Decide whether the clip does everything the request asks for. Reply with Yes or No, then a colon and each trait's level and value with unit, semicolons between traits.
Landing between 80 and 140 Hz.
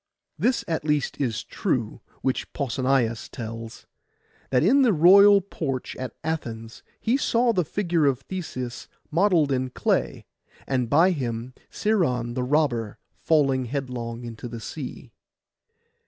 Yes: low, 135 Hz